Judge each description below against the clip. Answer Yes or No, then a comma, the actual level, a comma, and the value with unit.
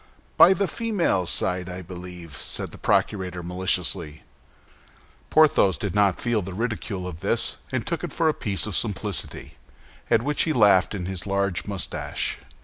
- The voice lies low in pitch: Yes, very low, 95 Hz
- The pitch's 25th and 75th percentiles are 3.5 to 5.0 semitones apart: Yes, average, 3.8 semitones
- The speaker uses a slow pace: No, average, 160 wpm